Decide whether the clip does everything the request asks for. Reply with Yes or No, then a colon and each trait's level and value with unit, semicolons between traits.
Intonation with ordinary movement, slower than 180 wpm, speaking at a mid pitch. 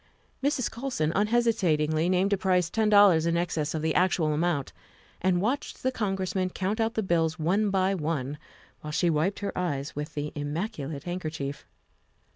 Yes: average, 4.5 semitones; average, 170 wpm; medium, 175 Hz